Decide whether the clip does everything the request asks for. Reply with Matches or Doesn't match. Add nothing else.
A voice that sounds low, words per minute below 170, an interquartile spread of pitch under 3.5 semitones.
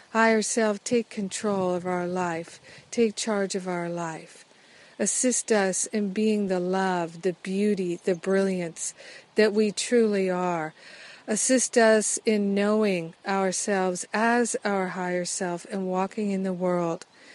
Doesn't match